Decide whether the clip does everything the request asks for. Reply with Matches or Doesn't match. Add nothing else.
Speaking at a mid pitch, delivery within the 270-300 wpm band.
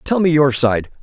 Doesn't match